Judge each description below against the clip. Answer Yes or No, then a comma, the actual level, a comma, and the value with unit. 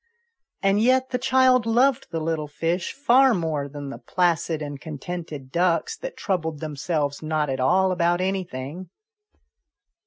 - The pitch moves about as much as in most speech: Yes, average, 5.0 semitones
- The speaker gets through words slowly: No, average, 145 wpm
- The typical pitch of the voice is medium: Yes, medium, 170 Hz